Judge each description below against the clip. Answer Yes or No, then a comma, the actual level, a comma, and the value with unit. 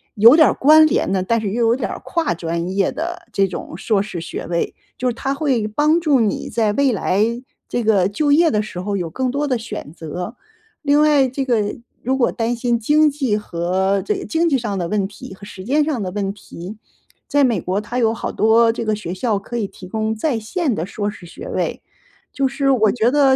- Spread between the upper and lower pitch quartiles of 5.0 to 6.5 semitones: Yes, wide, 5.6 semitones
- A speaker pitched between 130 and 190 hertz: No, high, 225 Hz